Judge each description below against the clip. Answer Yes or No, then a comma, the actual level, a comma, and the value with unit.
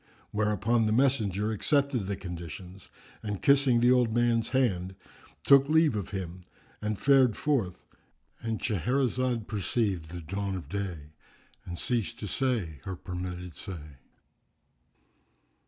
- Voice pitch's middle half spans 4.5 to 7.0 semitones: Yes, average, 5.2 semitones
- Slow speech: Yes, slow, 125 wpm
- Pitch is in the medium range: No, low, 105 Hz